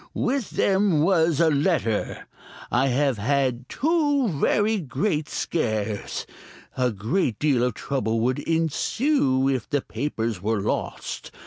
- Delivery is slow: Yes, slow, 130 wpm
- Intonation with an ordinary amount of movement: No, wide, 6.4 semitones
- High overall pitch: No, medium, 140 Hz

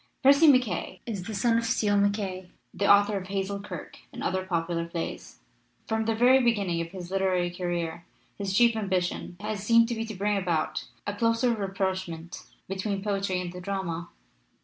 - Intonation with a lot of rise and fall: No, average, 3.2 semitones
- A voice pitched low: No, high, 195 Hz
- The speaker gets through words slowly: No, average, 175 wpm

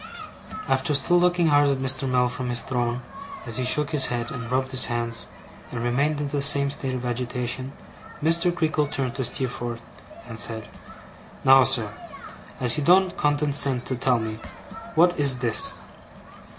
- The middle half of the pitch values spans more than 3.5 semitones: No, average, 3.0 semitones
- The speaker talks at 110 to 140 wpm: No, average, 165 wpm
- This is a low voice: Yes, low, 130 Hz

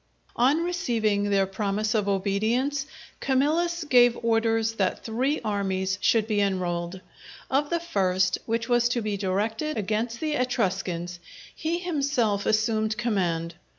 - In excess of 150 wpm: No, slow, 135 wpm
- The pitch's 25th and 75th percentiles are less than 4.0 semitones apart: No, average, 4.5 semitones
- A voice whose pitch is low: No, high, 220 Hz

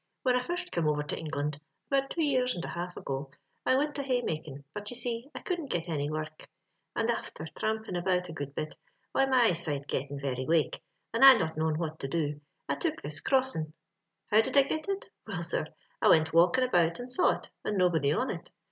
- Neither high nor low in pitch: Yes, medium, 175 Hz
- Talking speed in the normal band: No, fast, 225 wpm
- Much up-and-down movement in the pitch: Yes, wide, 8.7 semitones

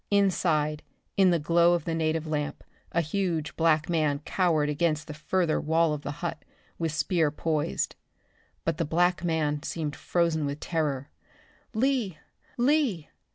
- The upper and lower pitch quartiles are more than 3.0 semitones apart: No, narrow, 2.4 semitones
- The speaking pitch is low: No, medium, 160 Hz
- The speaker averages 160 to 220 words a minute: No, average, 150 wpm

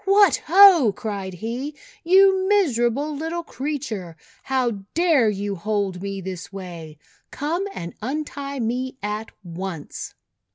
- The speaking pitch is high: Yes, high, 240 Hz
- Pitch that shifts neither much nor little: No, wide, 7.8 semitones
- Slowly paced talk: Yes, slow, 120 wpm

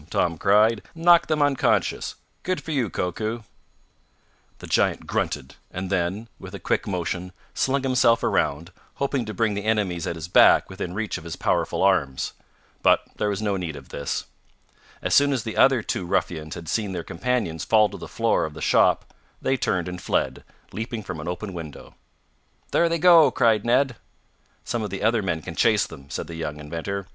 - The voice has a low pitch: Yes, low, 100 Hz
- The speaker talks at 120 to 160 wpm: No, average, 190 wpm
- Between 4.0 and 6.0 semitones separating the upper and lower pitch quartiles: Yes, wide, 5.5 semitones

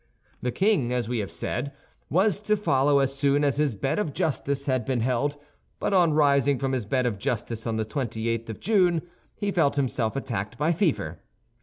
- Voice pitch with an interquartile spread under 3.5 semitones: No, average, 4.3 semitones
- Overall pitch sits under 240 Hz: Yes, low, 135 Hz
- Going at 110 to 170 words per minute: No, average, 200 wpm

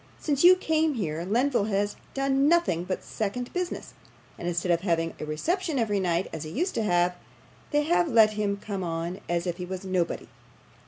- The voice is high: Yes, high, 200 Hz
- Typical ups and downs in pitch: No, wide, 7.9 semitones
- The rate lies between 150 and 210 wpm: Yes, average, 195 wpm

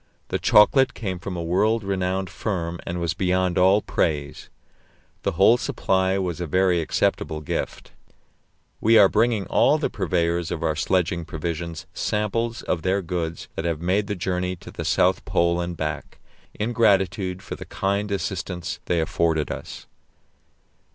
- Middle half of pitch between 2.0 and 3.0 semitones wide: Yes, average, 2.7 semitones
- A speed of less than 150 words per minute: No, average, 160 wpm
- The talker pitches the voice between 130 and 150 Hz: No, very low, 90 Hz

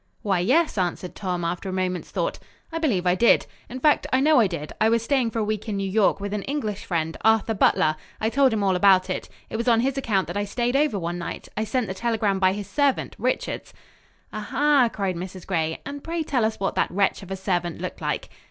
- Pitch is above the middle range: Yes, high, 205 Hz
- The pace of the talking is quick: Yes, fast, 245 wpm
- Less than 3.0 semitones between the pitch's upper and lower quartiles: No, average, 4.7 semitones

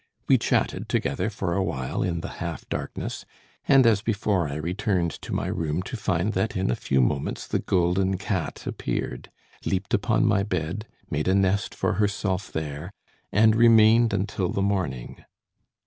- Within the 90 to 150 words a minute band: No, average, 165 wpm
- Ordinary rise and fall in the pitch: Yes, average, 3.7 semitones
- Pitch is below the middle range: Yes, very low, 95 Hz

